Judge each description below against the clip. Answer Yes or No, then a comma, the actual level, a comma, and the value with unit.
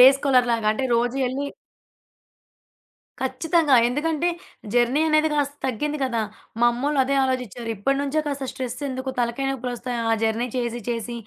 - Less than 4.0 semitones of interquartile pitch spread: Yes, average, 2.9 semitones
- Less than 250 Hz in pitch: No, very high, 260 Hz